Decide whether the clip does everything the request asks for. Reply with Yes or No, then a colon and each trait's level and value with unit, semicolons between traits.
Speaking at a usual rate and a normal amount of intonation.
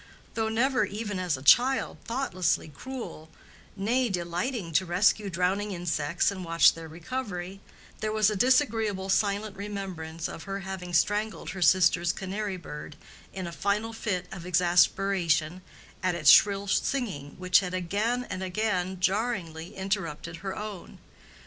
Yes: average, 145 wpm; average, 3.4 semitones